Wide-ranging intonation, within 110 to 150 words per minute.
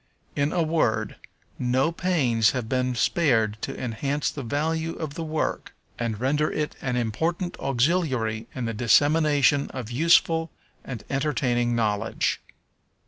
No: average, 4.8 semitones; slow, 135 wpm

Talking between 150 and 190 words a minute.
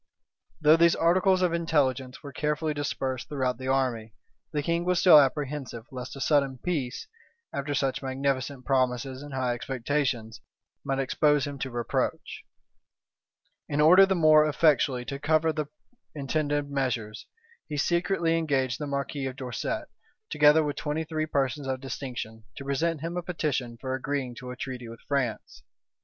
Yes: average, 155 wpm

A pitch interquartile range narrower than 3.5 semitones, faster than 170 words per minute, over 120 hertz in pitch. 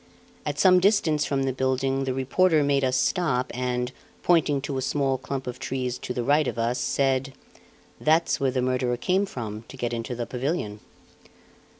Yes: average, 2.8 semitones; average, 185 wpm; low, 135 Hz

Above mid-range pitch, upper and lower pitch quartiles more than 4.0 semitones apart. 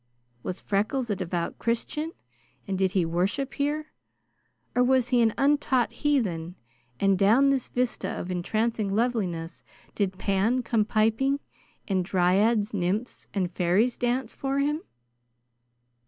Yes: high, 220 Hz; average, 5.1 semitones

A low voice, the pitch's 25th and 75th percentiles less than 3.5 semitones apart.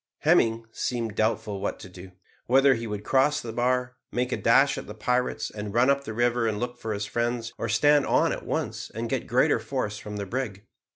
Yes: low, 115 Hz; average, 2.9 semitones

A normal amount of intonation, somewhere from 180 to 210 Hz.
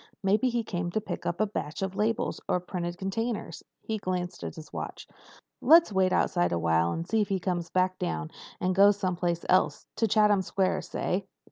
Yes: average, 3.1 semitones; medium, 185 Hz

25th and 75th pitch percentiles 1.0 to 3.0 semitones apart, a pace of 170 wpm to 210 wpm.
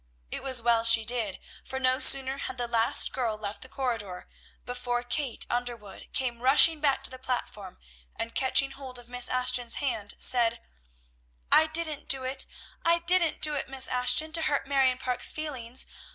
Yes: narrow, 2.4 semitones; average, 175 wpm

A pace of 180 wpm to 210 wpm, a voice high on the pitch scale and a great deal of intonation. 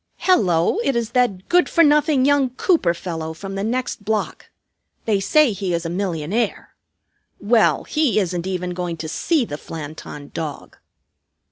No: average, 155 wpm; high, 195 Hz; wide, 7.1 semitones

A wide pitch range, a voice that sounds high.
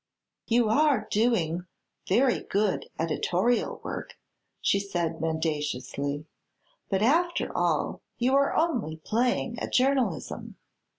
Yes: wide, 7.4 semitones; high, 210 Hz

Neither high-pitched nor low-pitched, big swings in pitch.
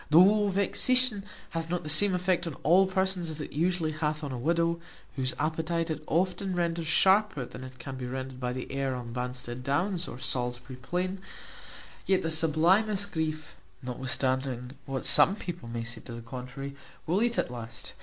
Yes: medium, 155 Hz; wide, 5.9 semitones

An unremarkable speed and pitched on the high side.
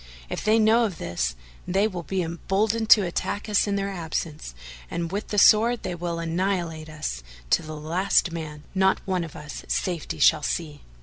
No: average, 185 wpm; medium, 175 Hz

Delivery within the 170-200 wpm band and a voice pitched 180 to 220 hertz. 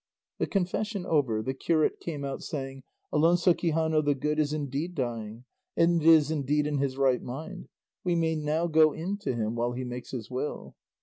No: average, 185 wpm; medium, 150 Hz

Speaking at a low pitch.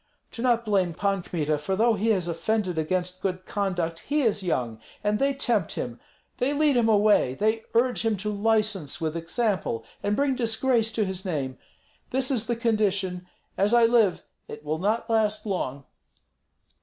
No: high, 205 Hz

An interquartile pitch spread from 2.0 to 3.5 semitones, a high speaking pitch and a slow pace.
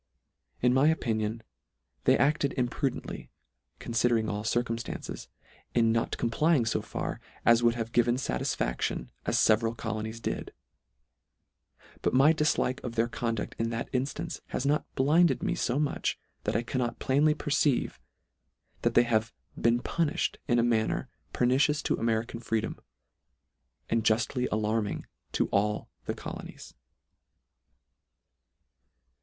No: average, 3.0 semitones; low, 120 Hz; slow, 125 wpm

